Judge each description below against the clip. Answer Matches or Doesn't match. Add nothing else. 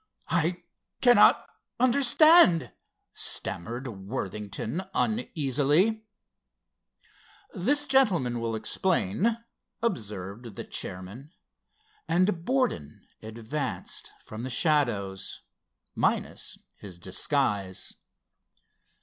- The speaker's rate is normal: Doesn't match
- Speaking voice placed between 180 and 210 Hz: Doesn't match